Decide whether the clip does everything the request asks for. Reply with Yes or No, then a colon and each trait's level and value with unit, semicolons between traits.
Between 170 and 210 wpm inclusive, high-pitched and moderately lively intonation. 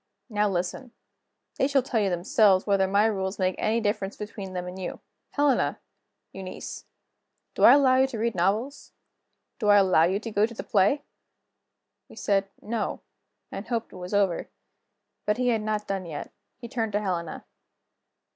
Yes: average, 175 wpm; high, 205 Hz; average, 3.3 semitones